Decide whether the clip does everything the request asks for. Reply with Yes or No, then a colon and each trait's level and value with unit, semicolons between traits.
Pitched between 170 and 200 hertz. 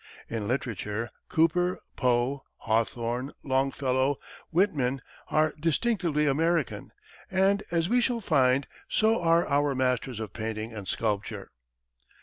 No: low, 135 Hz